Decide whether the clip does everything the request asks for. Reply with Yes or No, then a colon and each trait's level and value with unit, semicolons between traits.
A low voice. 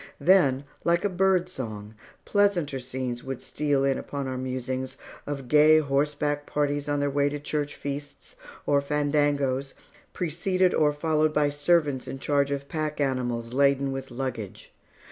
No: medium, 145 Hz